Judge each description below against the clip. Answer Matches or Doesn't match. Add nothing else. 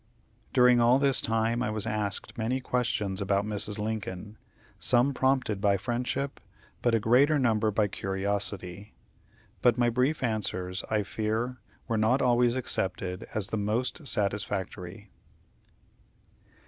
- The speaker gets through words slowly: Matches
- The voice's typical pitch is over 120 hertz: Doesn't match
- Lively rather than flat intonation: Doesn't match